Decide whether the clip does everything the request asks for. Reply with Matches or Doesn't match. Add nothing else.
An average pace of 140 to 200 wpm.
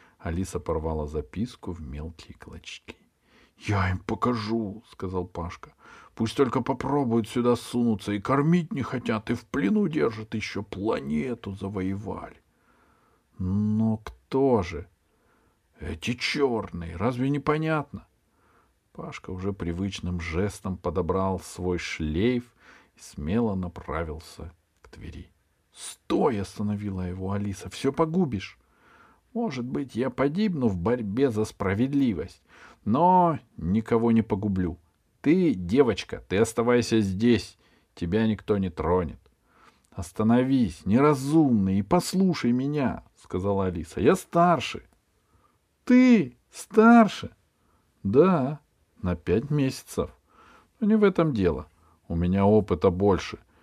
Doesn't match